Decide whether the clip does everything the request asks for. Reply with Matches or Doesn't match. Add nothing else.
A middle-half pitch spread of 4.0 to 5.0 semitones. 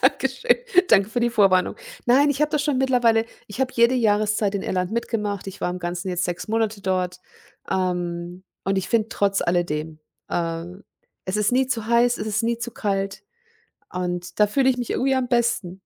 Matches